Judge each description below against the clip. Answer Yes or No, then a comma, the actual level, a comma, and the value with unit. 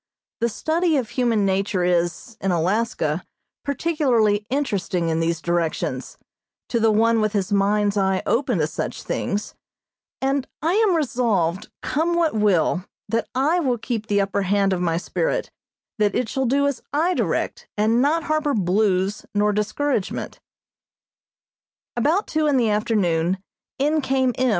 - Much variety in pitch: Yes, wide, 6.2 semitones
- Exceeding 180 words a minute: No, average, 150 wpm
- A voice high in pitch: Yes, high, 220 Hz